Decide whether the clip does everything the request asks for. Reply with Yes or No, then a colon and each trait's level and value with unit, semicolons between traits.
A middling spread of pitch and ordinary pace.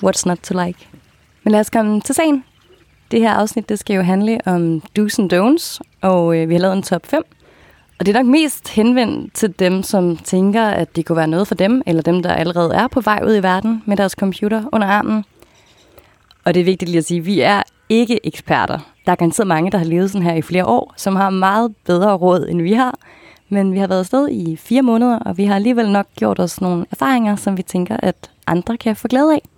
No: average, 3.8 semitones; fast, 240 wpm